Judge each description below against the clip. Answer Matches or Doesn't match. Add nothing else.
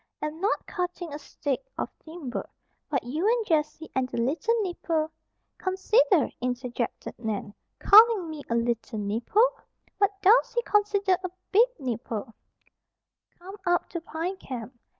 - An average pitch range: Doesn't match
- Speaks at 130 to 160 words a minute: Matches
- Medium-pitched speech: Doesn't match